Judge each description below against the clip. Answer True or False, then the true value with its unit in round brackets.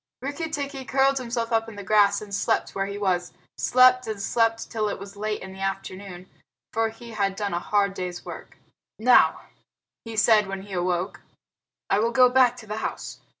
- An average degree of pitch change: True (3.3 semitones)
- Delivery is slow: False (195 wpm)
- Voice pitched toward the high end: True (215 Hz)